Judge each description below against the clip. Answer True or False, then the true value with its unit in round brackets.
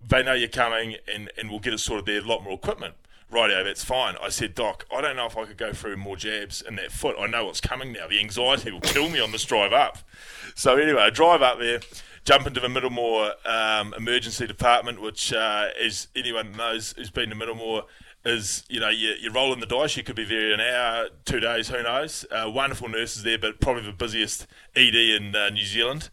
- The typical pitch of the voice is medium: False (115 Hz)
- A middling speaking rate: False (230 wpm)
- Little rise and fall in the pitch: True (2.3 semitones)